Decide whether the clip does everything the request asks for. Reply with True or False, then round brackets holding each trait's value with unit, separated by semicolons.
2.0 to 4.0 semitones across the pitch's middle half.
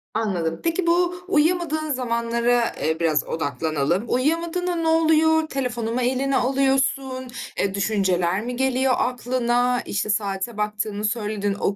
False (5.0 semitones)